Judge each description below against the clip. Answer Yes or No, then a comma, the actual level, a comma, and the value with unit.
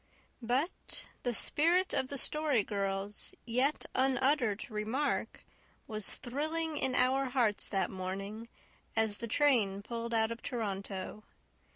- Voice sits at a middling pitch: No, high, 235 Hz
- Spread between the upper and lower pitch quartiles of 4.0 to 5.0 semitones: Yes, average, 4.6 semitones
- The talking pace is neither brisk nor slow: No, slow, 125 wpm